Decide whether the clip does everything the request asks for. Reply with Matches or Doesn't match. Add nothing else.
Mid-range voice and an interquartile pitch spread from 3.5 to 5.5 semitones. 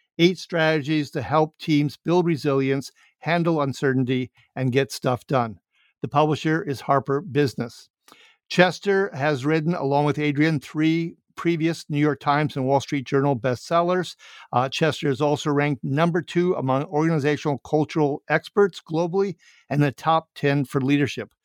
Doesn't match